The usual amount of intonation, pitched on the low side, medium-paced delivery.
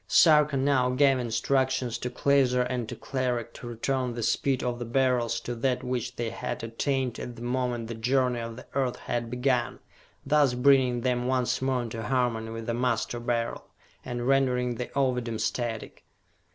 No: narrow, 1.8 semitones; low, 125 Hz; average, 175 wpm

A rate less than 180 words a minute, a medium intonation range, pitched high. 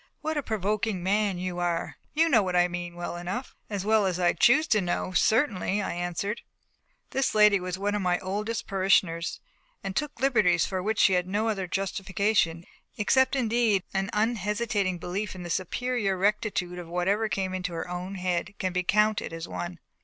No: average, 185 wpm; average, 3.1 semitones; high, 195 Hz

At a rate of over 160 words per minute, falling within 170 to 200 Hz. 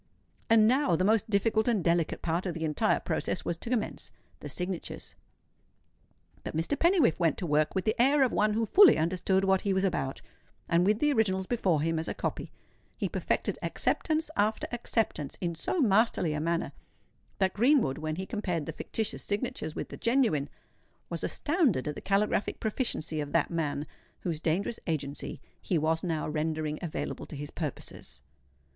Yes: average, 175 wpm; medium, 185 Hz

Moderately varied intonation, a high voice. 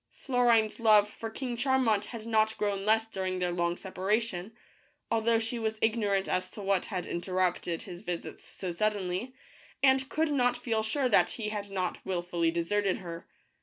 Yes: average, 3.8 semitones; high, 210 Hz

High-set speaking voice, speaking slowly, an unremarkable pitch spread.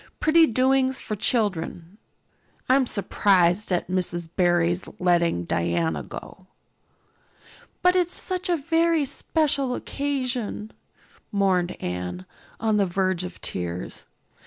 No: high, 195 Hz; slow, 110 wpm; wide, 7.4 semitones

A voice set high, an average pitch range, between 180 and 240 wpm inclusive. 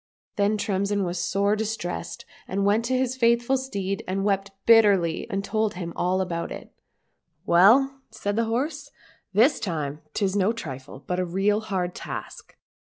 No: high, 200 Hz; average, 3.7 semitones; average, 170 wpm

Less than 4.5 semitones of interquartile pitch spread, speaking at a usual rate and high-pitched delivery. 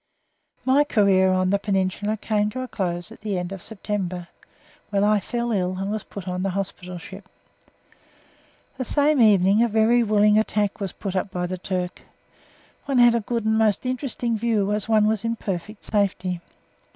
Yes: average, 2.9 semitones; average, 185 wpm; high, 205 Hz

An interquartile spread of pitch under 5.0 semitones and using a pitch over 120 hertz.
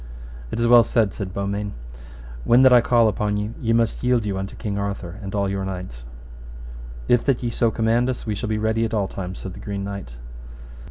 No: average, 2.8 semitones; low, 105 Hz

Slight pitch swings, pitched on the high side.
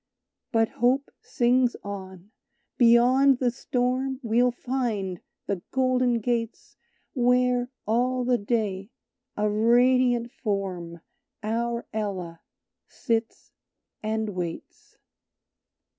No: average, 3.2 semitones; high, 235 Hz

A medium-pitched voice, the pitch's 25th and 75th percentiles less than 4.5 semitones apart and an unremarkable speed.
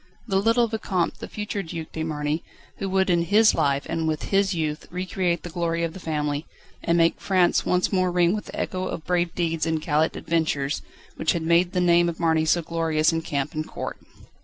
No: medium, 170 Hz; narrow, 2.4 semitones; fast, 210 wpm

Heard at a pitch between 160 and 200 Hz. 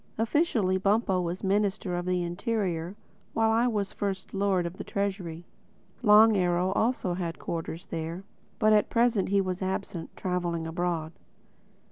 Yes: high, 190 Hz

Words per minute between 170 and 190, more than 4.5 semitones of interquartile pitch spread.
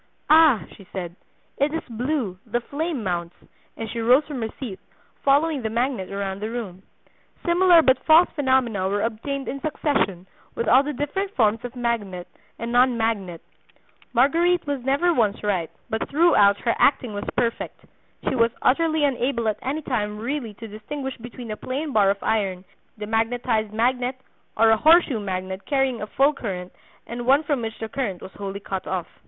Yes: average, 175 wpm; average, 5.0 semitones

